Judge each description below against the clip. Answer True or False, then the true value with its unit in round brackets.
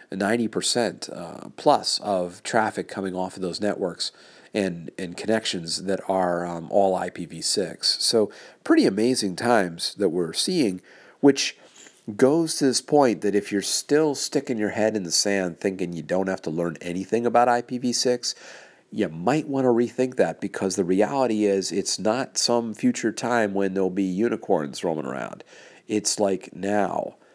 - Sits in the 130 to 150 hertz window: False (105 Hz)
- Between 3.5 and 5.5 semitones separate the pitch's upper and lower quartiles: True (4.5 semitones)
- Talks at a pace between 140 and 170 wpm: True (160 wpm)